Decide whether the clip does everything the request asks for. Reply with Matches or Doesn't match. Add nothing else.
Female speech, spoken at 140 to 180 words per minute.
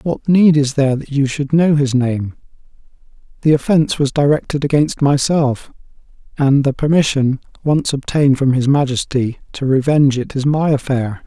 Doesn't match